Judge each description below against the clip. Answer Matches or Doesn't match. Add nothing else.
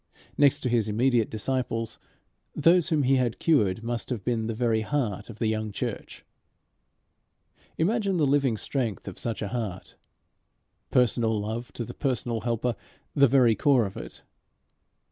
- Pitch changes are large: Doesn't match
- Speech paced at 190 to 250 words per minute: Doesn't match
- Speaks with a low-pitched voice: Matches